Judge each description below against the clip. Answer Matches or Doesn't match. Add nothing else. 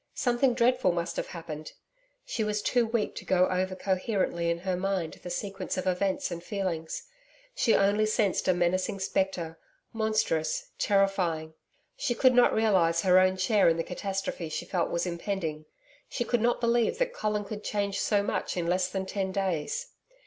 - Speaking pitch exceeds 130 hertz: Matches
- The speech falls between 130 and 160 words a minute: Doesn't match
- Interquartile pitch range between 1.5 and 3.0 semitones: Doesn't match